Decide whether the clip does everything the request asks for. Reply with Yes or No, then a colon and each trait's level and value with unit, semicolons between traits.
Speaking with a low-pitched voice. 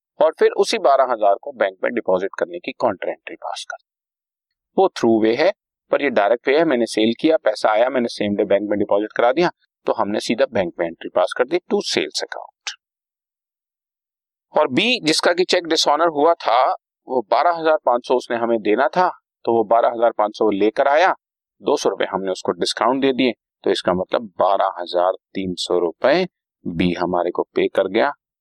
Yes: low, 120 Hz